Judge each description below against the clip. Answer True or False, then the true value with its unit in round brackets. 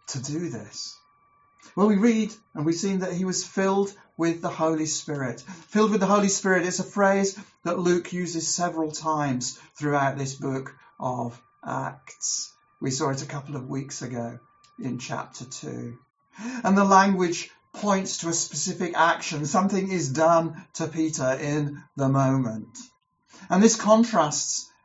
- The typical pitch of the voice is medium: True (165 Hz)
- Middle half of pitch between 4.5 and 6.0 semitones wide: True (4.9 semitones)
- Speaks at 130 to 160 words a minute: True (155 wpm)